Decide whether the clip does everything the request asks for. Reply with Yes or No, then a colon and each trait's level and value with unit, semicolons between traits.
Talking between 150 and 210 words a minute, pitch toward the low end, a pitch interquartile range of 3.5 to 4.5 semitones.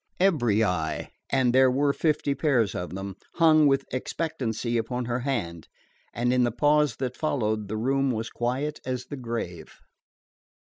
Yes: average, 155 wpm; low, 125 Hz; average, 4.0 semitones